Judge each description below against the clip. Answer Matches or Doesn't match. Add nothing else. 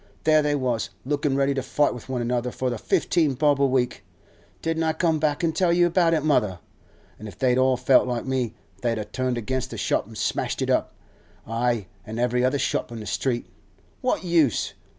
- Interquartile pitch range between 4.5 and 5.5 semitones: Doesn't match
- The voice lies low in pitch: Matches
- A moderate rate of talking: Doesn't match